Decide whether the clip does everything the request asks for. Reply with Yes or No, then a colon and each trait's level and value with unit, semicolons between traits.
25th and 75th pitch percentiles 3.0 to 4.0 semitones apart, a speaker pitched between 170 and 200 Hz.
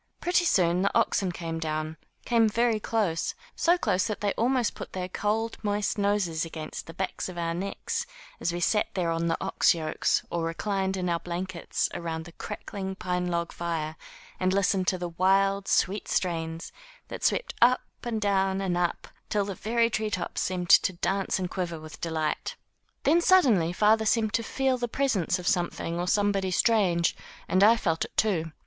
Yes: average, 3.7 semitones; medium, 185 Hz